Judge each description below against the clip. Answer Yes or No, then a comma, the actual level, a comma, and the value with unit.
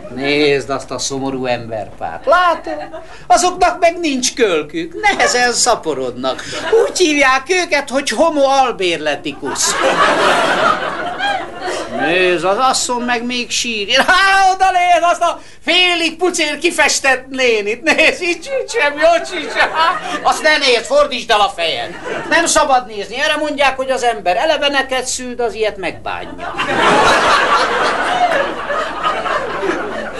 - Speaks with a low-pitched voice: No, very high, 285 Hz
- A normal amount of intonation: No, wide, 6.5 semitones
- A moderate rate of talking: Yes, average, 115 wpm